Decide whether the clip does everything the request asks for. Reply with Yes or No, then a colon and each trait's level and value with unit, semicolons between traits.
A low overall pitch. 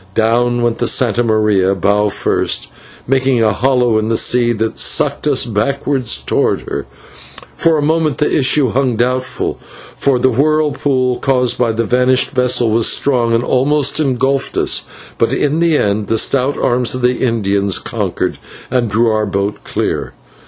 Yes: low, 125 Hz